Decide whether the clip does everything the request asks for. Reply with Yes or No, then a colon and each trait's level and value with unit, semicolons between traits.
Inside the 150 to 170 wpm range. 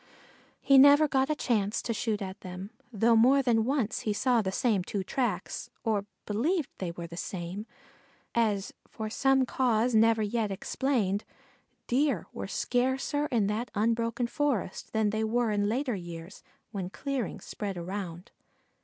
Yes: average, 160 wpm